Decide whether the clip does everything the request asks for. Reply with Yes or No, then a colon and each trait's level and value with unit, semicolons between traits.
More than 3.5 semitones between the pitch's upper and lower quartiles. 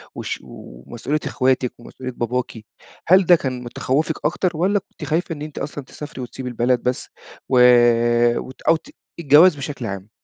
Yes: average, 4.2 semitones